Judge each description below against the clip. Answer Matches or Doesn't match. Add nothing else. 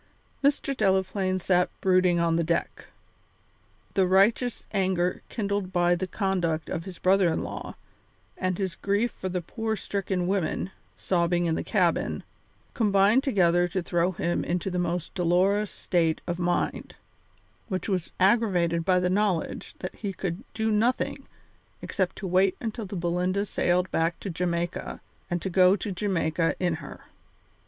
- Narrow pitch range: Matches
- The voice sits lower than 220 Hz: Matches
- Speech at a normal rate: Matches